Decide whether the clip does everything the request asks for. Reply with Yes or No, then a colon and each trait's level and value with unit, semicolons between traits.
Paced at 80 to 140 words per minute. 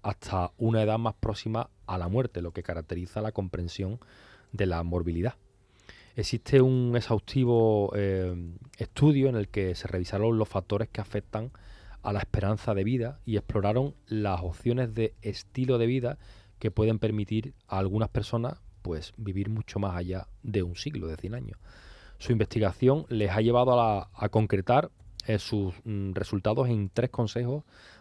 No: average, 165 wpm